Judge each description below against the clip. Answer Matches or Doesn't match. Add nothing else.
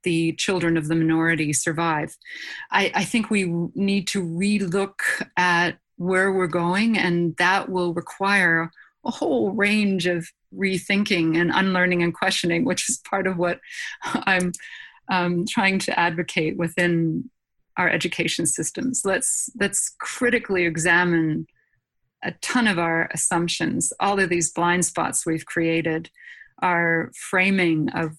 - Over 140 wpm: Doesn't match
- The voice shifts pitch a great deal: Doesn't match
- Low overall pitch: Doesn't match